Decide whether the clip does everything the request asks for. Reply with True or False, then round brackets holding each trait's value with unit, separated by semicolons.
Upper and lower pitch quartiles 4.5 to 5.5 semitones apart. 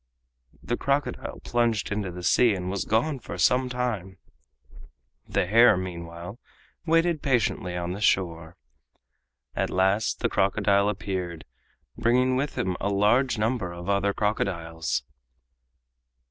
True (5.0 semitones)